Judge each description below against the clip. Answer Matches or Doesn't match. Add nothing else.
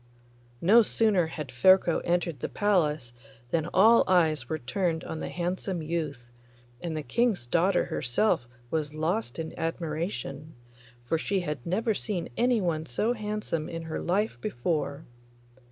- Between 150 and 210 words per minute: Doesn't match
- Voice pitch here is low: Doesn't match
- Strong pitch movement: Doesn't match